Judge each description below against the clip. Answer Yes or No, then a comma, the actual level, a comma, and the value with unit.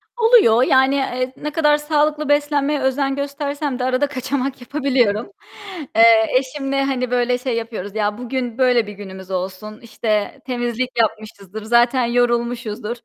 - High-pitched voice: Yes, very high, 250 Hz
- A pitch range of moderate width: Yes, average, 3.6 semitones